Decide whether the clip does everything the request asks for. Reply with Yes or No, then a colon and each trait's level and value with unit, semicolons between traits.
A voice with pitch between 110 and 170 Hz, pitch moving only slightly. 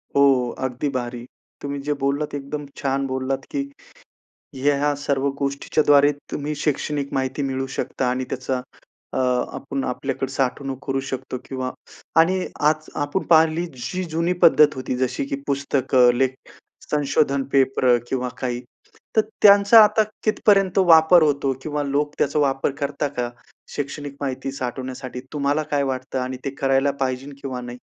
Yes: medium, 140 Hz; narrow, 2.1 semitones